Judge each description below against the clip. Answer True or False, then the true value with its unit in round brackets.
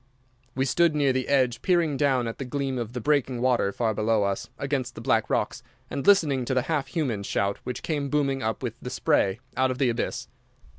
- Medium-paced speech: False (215 wpm)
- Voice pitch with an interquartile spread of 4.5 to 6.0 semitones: False (3.0 semitones)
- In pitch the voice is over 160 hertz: False (130 Hz)